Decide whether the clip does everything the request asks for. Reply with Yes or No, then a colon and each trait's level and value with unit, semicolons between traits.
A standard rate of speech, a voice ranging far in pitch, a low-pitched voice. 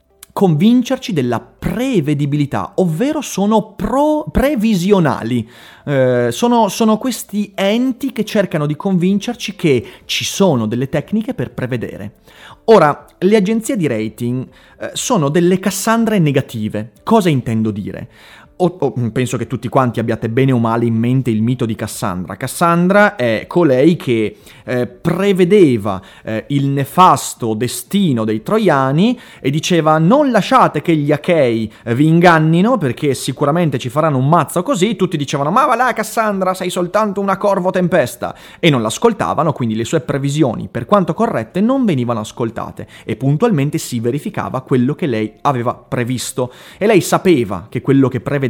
No: average, 145 wpm; wide, 8.4 semitones; medium, 150 Hz